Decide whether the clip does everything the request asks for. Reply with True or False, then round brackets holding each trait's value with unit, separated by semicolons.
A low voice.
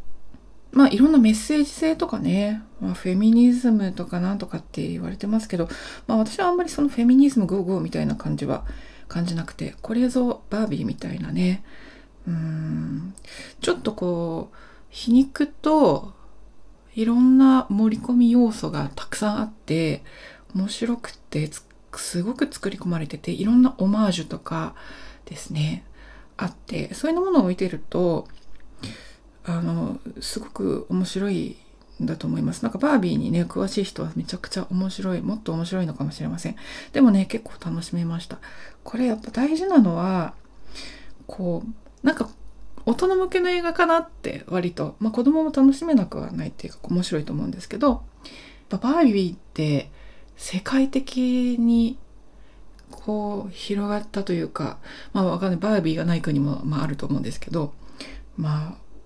False (210 Hz)